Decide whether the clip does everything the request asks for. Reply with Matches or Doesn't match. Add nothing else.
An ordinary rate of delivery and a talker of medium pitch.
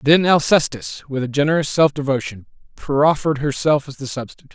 Matches